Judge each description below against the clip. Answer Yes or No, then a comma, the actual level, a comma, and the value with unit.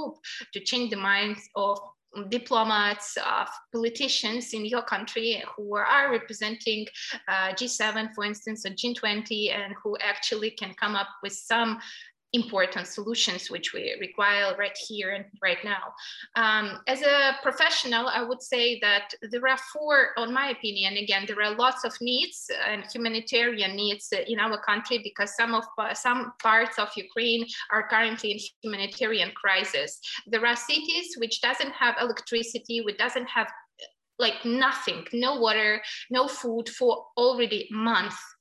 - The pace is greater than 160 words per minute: No, average, 150 wpm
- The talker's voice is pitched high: Yes, high, 225 Hz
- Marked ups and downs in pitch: No, average, 3.0 semitones